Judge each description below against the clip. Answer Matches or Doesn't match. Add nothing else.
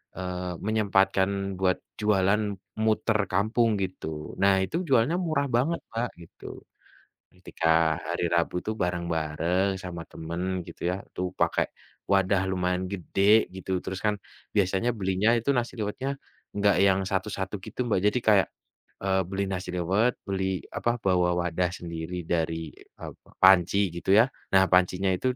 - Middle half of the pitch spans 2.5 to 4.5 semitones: Matches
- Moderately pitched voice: Doesn't match